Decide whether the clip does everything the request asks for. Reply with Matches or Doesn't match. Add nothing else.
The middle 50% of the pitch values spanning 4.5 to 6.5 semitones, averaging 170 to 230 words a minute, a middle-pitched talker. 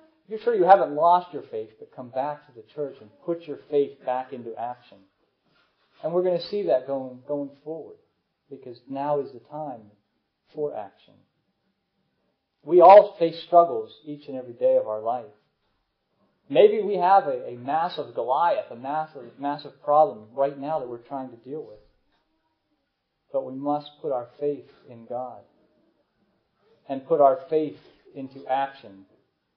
Doesn't match